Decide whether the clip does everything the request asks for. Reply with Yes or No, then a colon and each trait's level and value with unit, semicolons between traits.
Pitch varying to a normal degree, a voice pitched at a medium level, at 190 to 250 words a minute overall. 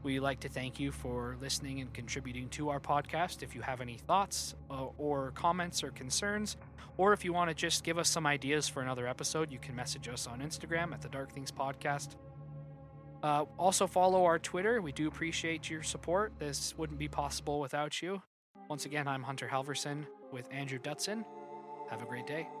Yes: average, 3.0 semitones; medium, 145 Hz; average, 195 wpm